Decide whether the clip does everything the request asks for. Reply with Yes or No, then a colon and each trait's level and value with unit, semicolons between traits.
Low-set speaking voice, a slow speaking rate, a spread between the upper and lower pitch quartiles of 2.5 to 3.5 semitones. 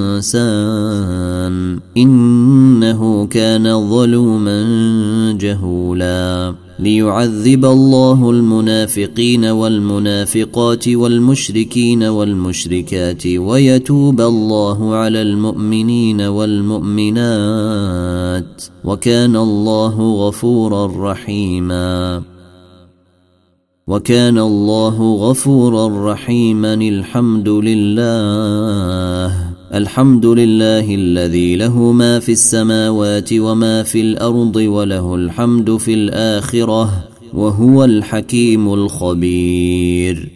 Yes: low, 110 Hz; slow, 60 wpm; average, 2.9 semitones